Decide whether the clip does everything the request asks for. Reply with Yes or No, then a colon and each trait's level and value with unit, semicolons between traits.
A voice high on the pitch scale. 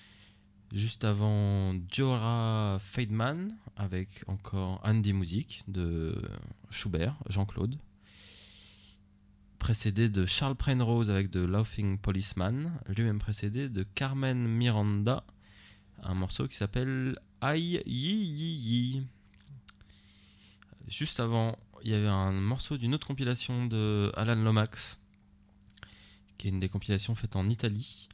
No: low, 105 Hz